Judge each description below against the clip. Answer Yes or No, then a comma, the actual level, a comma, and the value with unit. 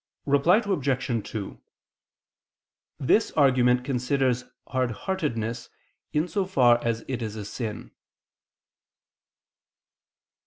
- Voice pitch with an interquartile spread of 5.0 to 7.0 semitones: No, average, 3.4 semitones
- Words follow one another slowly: Yes, slow, 85 wpm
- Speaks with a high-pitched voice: No, low, 125 Hz